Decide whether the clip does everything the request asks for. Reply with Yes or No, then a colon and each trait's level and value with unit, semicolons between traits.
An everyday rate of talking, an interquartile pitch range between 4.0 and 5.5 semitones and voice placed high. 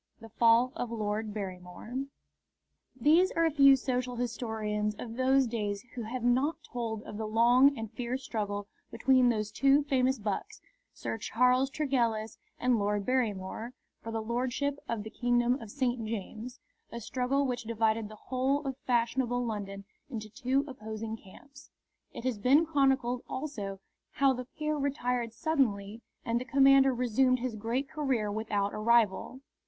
No: average, 155 wpm; average, 3.3 semitones; high, 240 Hz